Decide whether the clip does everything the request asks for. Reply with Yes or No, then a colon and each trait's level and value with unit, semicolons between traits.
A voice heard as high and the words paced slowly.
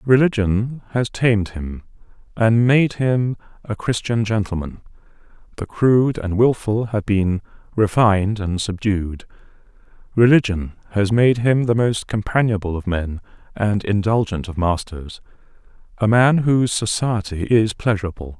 No: low, 105 Hz; slow, 120 wpm